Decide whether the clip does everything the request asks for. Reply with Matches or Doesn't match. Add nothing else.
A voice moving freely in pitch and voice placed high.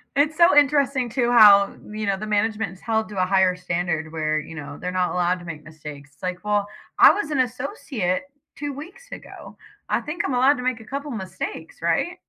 Matches